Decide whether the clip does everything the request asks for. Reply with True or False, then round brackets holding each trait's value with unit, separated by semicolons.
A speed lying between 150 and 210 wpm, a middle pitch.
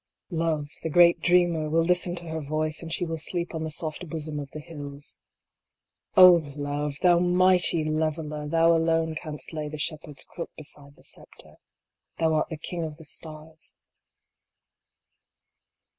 True (160 wpm; 160 Hz)